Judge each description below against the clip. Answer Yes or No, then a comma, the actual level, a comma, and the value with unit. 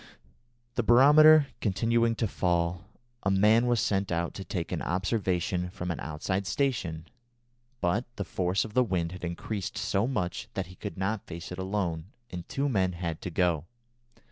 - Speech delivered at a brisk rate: No, average, 170 wpm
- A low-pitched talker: Yes, very low, 95 Hz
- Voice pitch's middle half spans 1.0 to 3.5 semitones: No, average, 4.1 semitones